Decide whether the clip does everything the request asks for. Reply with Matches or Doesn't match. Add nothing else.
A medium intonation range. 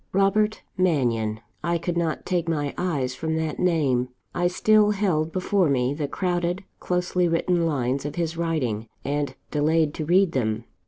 Matches